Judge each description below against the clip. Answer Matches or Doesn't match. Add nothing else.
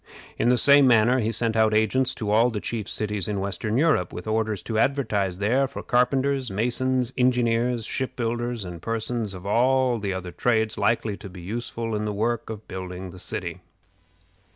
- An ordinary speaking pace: Matches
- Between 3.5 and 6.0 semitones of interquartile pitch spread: Doesn't match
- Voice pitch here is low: Matches